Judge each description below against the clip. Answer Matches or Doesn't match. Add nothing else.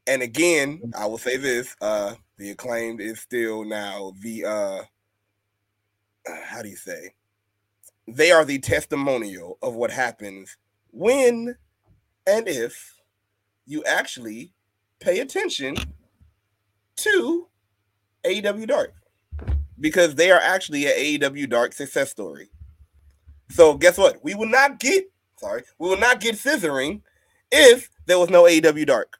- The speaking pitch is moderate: Doesn't match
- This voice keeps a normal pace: Doesn't match